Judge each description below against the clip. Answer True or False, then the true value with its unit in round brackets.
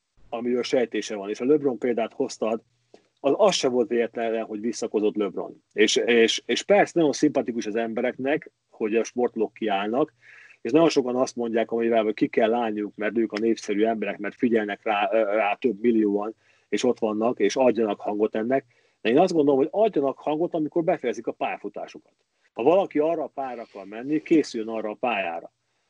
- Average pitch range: True (3.7 semitones)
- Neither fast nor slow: False (175 wpm)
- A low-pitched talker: True (120 Hz)